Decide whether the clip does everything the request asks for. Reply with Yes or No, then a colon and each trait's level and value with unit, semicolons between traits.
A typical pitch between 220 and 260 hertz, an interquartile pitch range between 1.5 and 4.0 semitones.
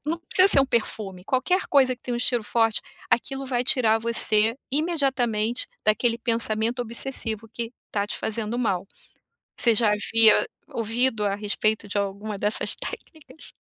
Yes: high, 230 Hz; average, 2.9 semitones